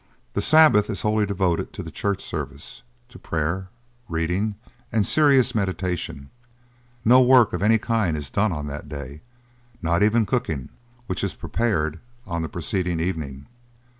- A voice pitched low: Yes, very low, 95 Hz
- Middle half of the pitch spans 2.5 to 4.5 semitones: No, wide, 5.5 semitones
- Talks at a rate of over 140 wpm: Yes, average, 150 wpm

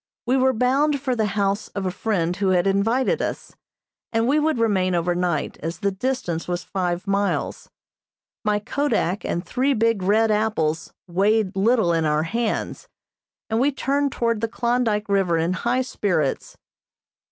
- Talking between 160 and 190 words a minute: Yes, average, 165 wpm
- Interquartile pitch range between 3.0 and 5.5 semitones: Yes, average, 5.0 semitones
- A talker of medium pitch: No, high, 210 Hz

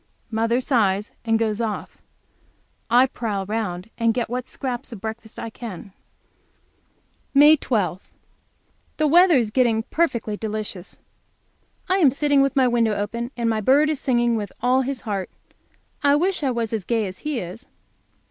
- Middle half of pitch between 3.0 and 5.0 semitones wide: Yes, average, 3.6 semitones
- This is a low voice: No, high, 235 Hz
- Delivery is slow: No, average, 160 wpm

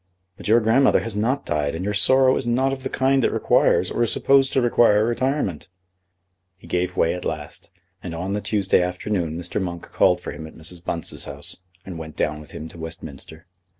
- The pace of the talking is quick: Yes, fast, 210 wpm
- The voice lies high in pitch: No, very low, 95 Hz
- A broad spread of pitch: Yes, wide, 6.2 semitones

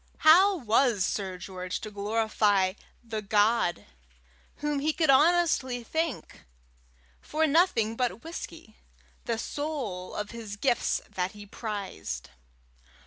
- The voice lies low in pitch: No, high, 225 Hz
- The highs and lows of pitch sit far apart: Yes, wide, 6.4 semitones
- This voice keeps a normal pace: No, slow, 115 wpm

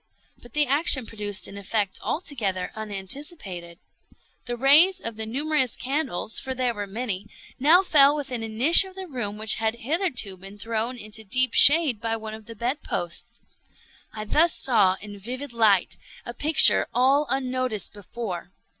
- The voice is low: No, high, 235 Hz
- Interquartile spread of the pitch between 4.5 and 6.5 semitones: Yes, average, 5.0 semitones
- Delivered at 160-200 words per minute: Yes, average, 165 wpm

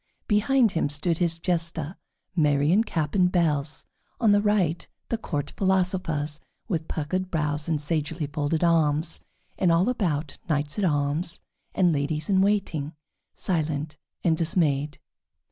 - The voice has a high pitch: No, medium, 165 Hz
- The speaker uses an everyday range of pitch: Yes, average, 3.7 semitones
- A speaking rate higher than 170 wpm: No, average, 140 wpm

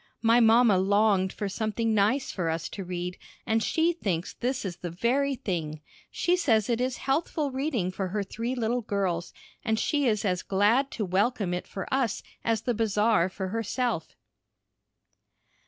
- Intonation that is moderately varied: Yes, average, 4.5 semitones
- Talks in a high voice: Yes, high, 220 Hz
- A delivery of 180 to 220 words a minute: No, average, 170 wpm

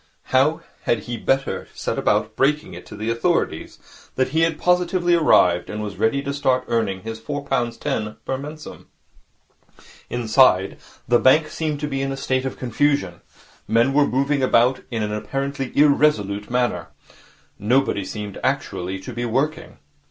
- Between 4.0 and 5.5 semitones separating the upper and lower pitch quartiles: Yes, average, 4.6 semitones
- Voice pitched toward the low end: Yes, low, 130 Hz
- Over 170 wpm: No, average, 165 wpm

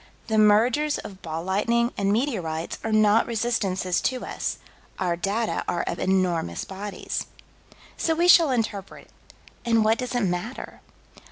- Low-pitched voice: No, high, 210 Hz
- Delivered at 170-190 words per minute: No, average, 145 wpm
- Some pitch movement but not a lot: Yes, average, 4.2 semitones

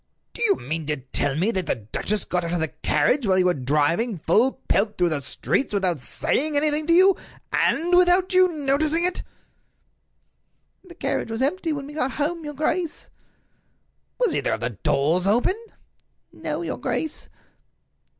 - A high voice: Yes, very high, 255 Hz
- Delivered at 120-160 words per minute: No, average, 170 wpm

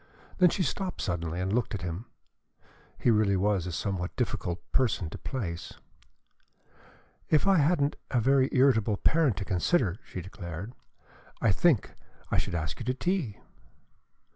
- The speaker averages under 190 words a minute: Yes, average, 150 wpm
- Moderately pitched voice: No, low, 105 Hz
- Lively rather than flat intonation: Yes, wide, 7.1 semitones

